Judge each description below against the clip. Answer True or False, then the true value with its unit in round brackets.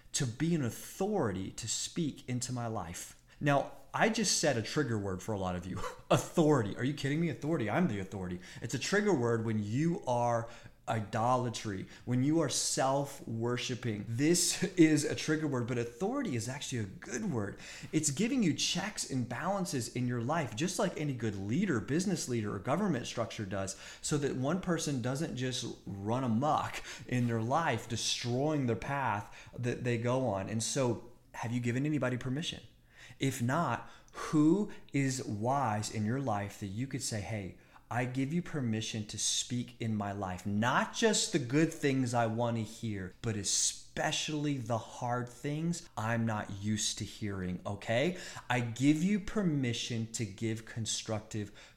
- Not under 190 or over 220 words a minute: False (175 wpm)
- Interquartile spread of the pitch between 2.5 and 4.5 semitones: False (5.1 semitones)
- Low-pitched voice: True (125 Hz)